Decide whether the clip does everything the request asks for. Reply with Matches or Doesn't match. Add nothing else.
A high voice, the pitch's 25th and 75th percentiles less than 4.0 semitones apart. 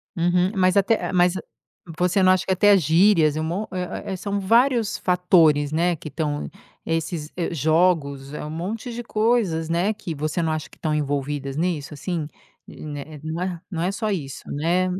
Doesn't match